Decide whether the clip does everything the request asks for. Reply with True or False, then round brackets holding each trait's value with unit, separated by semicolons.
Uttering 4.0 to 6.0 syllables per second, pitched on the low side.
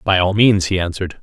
False (6.2 syllables/s; 95 Hz)